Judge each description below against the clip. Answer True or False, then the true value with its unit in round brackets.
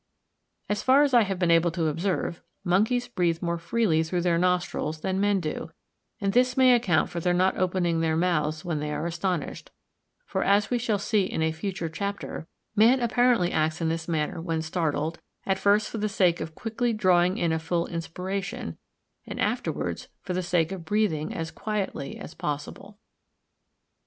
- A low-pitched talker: False (180 Hz)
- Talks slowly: False (180 wpm)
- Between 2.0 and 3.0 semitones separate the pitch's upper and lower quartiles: False (3.8 semitones)